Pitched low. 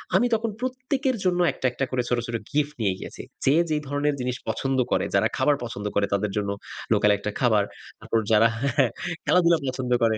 Yes: low, 130 Hz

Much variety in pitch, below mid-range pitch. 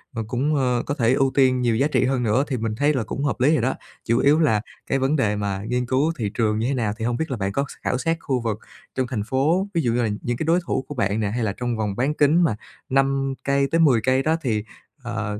No: average, 3.7 semitones; low, 130 Hz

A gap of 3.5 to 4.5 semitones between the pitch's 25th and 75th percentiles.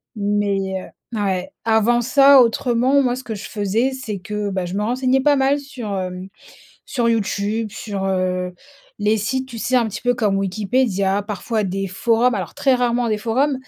Yes: average, 4.0 semitones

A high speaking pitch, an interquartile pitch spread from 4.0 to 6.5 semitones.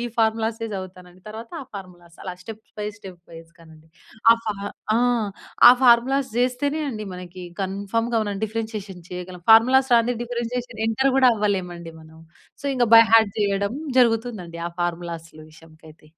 Yes: high, 210 Hz; average, 4.7 semitones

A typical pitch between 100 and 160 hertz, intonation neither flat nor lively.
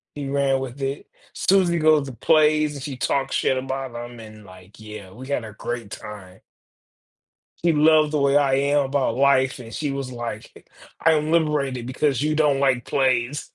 Yes: low, 135 Hz; average, 3.6 semitones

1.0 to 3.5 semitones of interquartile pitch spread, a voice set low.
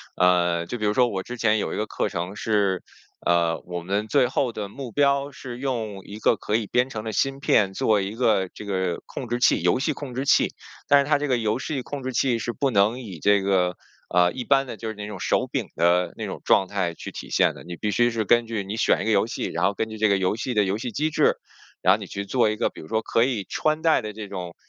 No: average, 4.3 semitones; low, 110 Hz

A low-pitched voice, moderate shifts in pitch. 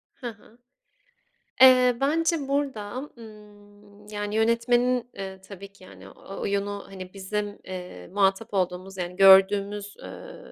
No: high, 205 Hz; average, 3.2 semitones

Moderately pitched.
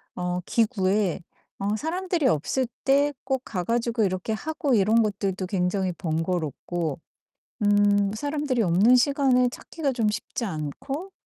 No: high, 215 Hz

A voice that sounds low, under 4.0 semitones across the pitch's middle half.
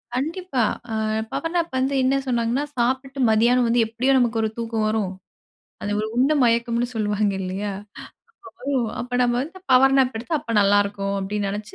No: high, 235 Hz; average, 3.6 semitones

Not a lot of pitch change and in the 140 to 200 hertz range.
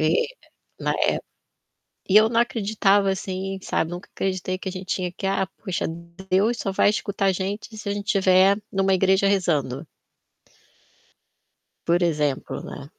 Yes: narrow, 2.1 semitones; high, 190 Hz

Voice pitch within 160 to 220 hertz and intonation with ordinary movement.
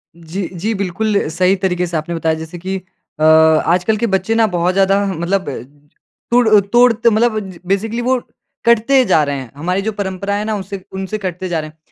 Yes: high, 190 Hz; average, 3.9 semitones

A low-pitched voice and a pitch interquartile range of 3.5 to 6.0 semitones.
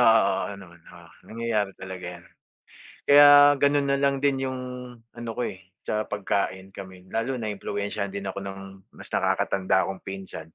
Yes: low, 100 Hz; average, 3.9 semitones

